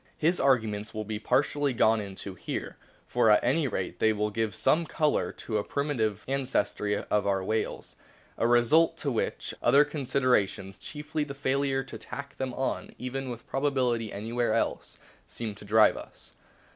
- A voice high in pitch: No, low, 120 Hz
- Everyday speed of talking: Yes, average, 170 wpm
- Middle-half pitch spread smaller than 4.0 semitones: No, average, 4.5 semitones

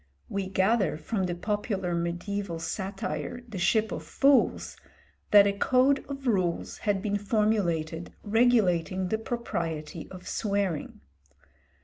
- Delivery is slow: Yes, slow, 120 wpm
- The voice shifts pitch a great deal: No, average, 4.1 semitones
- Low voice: No, high, 195 Hz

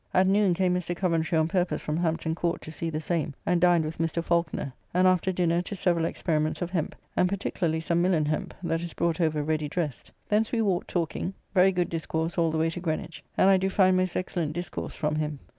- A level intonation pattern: Yes, narrow, 2.2 semitones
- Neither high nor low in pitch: Yes, medium, 170 Hz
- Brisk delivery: Yes, fast, 225 wpm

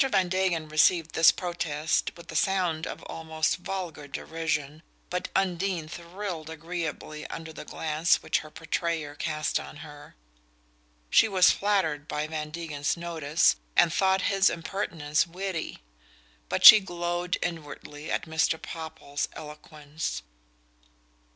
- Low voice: No, medium, 160 Hz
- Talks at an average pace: No, slow, 125 wpm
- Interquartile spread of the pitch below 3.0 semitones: Yes, narrow, 2.6 semitones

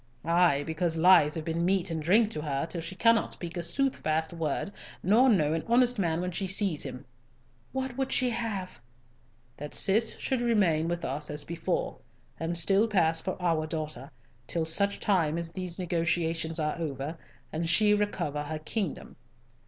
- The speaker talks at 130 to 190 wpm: Yes, average, 175 wpm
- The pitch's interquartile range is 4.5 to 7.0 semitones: No, average, 3.9 semitones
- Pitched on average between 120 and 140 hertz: No, medium, 170 Hz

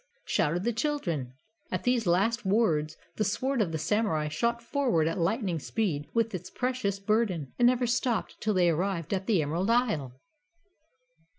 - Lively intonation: Yes, wide, 6.1 semitones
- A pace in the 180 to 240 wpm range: No, average, 165 wpm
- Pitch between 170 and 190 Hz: No, high, 200 Hz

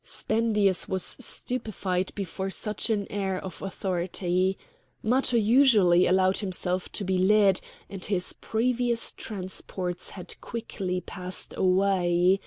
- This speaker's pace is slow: Yes, slow, 115 wpm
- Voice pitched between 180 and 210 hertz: Yes, high, 190 Hz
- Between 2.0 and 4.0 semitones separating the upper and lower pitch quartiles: Yes, average, 2.7 semitones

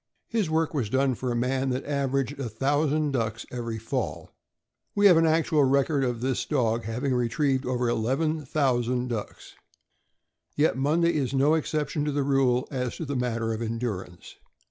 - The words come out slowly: No, average, 175 wpm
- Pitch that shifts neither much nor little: Yes, average, 3.4 semitones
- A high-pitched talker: No, low, 135 Hz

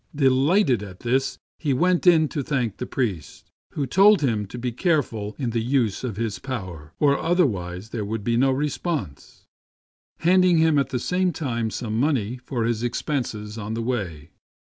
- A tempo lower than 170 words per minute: No, average, 175 wpm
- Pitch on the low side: Yes, low, 125 Hz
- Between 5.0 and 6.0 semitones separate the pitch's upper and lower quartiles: Yes, average, 5.3 semitones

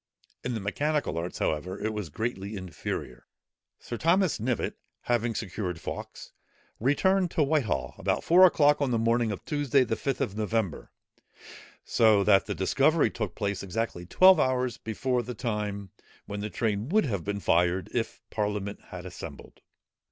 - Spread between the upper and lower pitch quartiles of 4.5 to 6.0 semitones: Yes, average, 4.8 semitones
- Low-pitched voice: Yes, low, 110 Hz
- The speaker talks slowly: No, average, 160 wpm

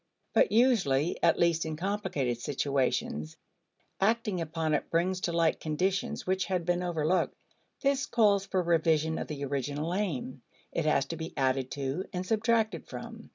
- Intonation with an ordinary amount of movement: Yes, average, 4.6 semitones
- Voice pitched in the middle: Yes, medium, 170 Hz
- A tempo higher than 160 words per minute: No, average, 155 wpm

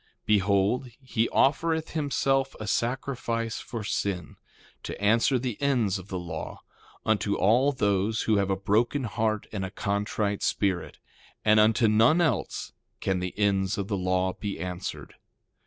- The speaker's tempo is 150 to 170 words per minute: Yes, average, 155 wpm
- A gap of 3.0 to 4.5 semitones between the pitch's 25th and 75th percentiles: Yes, average, 3.6 semitones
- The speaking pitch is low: Yes, low, 105 Hz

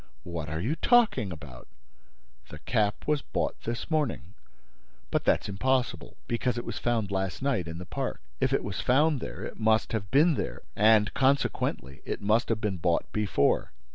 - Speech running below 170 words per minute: No, average, 175 wpm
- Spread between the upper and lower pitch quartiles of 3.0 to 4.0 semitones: No, wide, 5.6 semitones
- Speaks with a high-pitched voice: No, low, 110 Hz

